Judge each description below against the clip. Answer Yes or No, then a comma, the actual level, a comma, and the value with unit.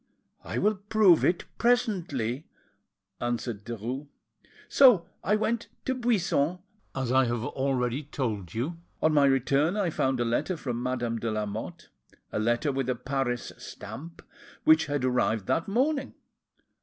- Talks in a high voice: No, low, 135 Hz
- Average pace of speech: Yes, average, 145 wpm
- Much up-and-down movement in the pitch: Yes, wide, 6.6 semitones